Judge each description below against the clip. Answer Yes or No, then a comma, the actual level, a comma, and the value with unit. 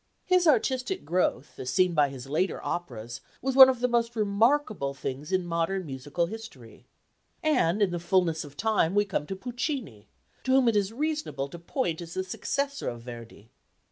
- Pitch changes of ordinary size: No, wide, 8.8 semitones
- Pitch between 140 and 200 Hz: Yes, medium, 185 Hz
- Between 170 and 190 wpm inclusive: Yes, average, 180 wpm